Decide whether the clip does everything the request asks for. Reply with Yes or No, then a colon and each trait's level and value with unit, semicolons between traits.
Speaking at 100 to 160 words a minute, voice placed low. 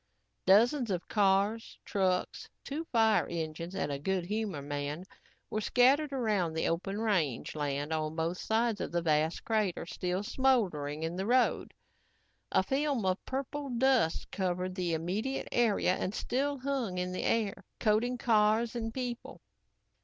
No: average, 150 wpm; high, 200 Hz